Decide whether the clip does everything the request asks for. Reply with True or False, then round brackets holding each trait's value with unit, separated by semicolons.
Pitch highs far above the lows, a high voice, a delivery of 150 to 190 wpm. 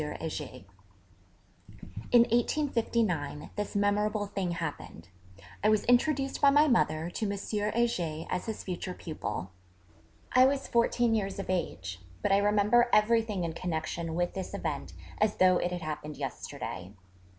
False (5.8 semitones; 200 Hz; 140 wpm)